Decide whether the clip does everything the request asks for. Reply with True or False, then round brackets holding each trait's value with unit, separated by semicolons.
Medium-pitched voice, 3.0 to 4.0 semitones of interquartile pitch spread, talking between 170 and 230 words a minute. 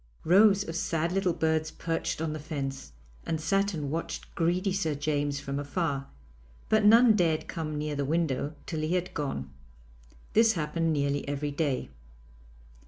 False (160 Hz; 3.4 semitones; 160 wpm)